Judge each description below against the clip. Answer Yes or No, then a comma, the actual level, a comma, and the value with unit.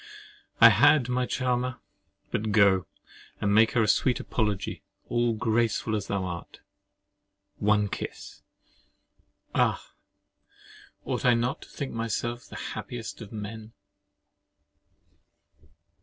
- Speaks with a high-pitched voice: No, low, 110 Hz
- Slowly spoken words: Yes, slow, 110 wpm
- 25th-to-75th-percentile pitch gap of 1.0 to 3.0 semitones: Yes, average, 2.7 semitones